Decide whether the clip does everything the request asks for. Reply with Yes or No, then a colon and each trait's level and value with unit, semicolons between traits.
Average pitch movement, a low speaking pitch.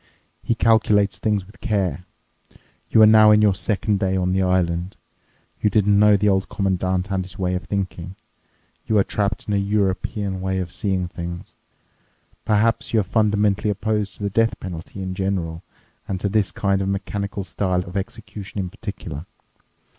No: narrow, 2.2 semitones; low, 100 Hz